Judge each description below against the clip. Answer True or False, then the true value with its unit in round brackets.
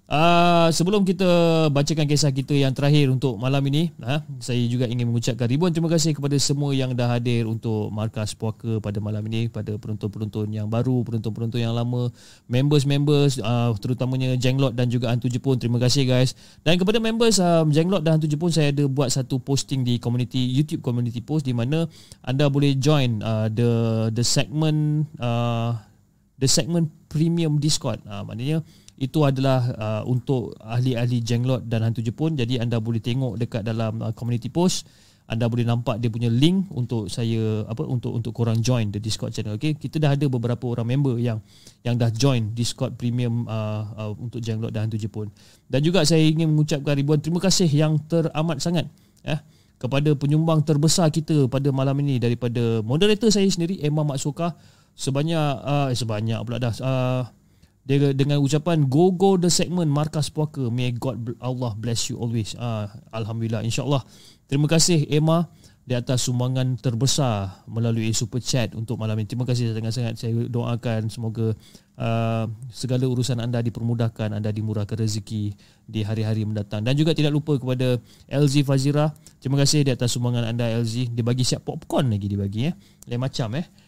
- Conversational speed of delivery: False (175 wpm)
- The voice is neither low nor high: False (125 Hz)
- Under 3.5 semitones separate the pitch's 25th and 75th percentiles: False (4.3 semitones)